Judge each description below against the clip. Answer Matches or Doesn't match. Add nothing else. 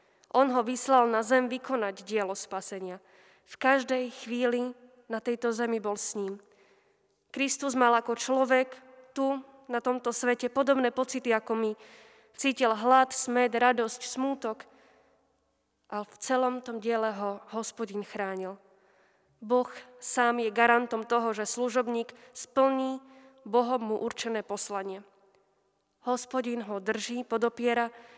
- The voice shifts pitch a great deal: Doesn't match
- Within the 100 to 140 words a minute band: Matches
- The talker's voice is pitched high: Matches